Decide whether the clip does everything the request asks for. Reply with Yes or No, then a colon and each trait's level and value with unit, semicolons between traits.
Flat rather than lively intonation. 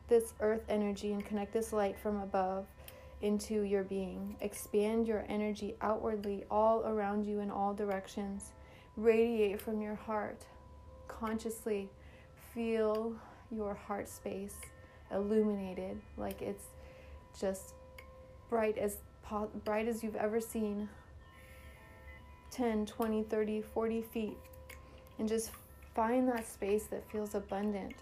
Yes: narrow, 2.2 semitones